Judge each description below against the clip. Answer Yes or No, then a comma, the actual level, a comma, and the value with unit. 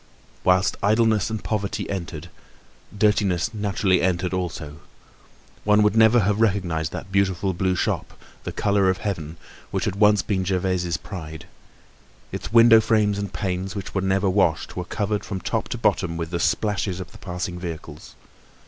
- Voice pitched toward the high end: No, very low, 95 Hz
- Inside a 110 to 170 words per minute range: Yes, average, 160 wpm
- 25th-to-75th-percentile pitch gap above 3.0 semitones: No, average, 2.7 semitones